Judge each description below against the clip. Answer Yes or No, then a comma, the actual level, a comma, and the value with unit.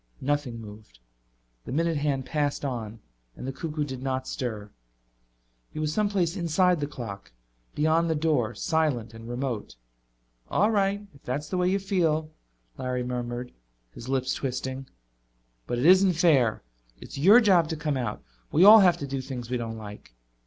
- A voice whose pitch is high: No, medium, 140 Hz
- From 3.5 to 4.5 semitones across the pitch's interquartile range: No, average, 5.2 semitones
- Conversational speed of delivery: Yes, average, 165 wpm